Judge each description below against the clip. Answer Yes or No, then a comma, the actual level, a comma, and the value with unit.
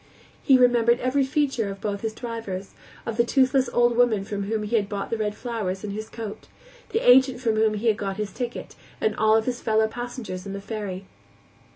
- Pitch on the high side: Yes, high, 220 Hz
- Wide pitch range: No, average, 2.9 semitones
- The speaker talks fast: Yes, fast, 215 wpm